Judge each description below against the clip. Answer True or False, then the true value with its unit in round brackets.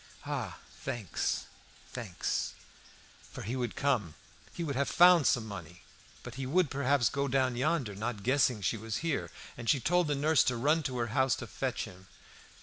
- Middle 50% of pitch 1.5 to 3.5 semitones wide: False (4.0 semitones)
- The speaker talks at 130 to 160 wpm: False (180 wpm)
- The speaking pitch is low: True (130 Hz)